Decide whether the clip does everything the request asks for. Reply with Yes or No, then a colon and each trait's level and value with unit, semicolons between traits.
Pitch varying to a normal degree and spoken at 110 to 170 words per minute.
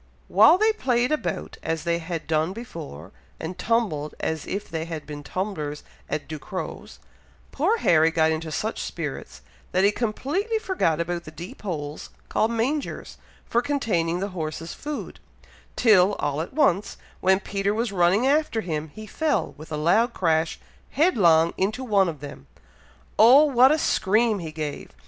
No: wide, 6.7 semitones; average, 160 wpm